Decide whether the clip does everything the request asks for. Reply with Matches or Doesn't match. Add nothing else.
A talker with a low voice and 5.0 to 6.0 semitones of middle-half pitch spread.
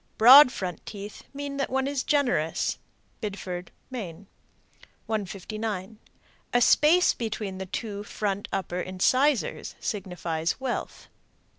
Doesn't match